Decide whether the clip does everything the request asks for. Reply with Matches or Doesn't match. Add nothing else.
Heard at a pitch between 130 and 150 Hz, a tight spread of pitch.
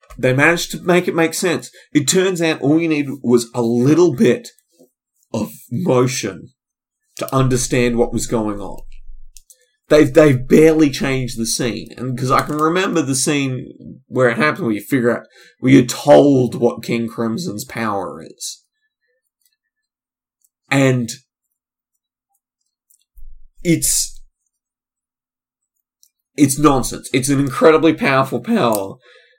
Doesn't match